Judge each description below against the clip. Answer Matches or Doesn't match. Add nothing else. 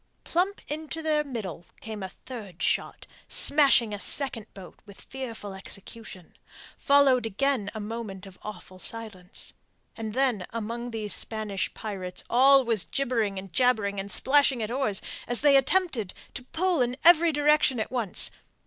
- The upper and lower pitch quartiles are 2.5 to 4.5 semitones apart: Doesn't match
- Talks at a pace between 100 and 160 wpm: Matches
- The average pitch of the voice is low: Doesn't match